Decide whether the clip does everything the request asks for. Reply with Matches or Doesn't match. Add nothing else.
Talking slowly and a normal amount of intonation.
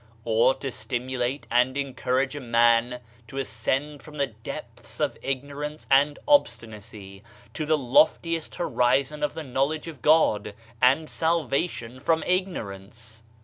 Matches